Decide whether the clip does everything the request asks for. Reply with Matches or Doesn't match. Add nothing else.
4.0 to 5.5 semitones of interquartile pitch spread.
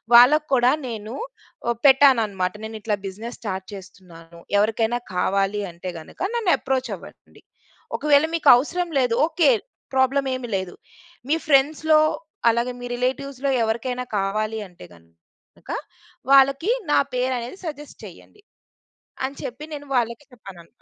Matches